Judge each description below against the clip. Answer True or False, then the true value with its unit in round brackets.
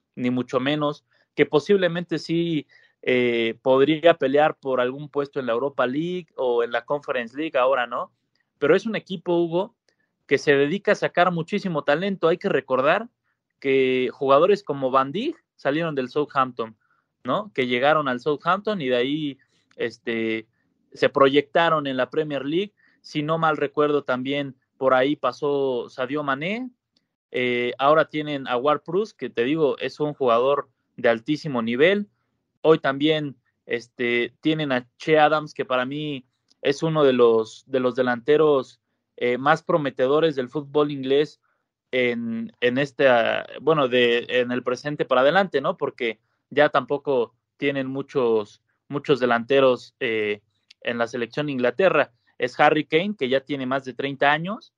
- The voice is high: False (140 Hz)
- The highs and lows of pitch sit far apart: False (3.6 semitones)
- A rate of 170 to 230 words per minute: False (155 wpm)